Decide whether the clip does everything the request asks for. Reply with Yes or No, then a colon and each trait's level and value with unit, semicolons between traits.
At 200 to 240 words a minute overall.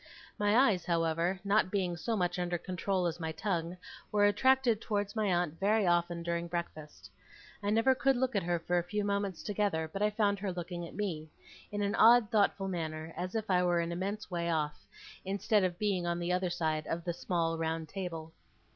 Yes: fast, 205 wpm